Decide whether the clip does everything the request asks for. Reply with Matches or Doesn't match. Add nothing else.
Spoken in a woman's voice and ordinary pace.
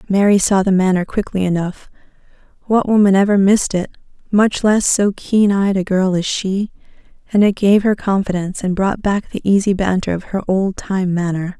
Matches